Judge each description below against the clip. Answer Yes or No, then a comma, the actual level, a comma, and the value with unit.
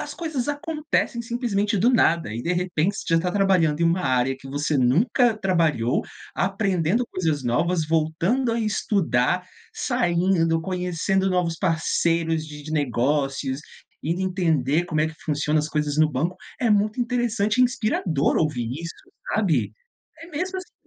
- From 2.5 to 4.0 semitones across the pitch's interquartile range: No, average, 5.3 semitones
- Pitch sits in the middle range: Yes, medium, 170 Hz